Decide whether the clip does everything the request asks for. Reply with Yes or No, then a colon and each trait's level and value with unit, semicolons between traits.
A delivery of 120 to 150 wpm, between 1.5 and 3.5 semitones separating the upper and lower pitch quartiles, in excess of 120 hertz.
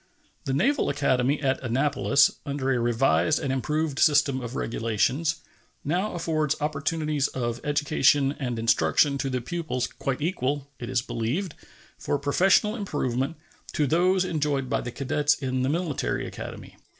Yes: average, 145 wpm; average, 3.2 semitones; medium, 140 Hz